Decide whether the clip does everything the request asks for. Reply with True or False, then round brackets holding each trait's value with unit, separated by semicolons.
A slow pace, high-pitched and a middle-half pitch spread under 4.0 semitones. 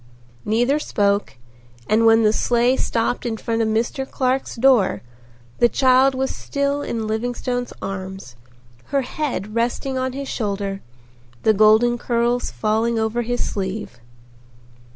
True (130 wpm; 235 Hz; 2.9 semitones)